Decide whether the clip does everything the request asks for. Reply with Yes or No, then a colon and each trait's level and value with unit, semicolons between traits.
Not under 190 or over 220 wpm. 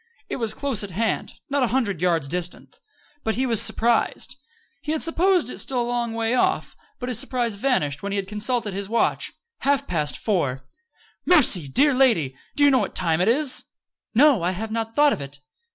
Yes: average, 200 wpm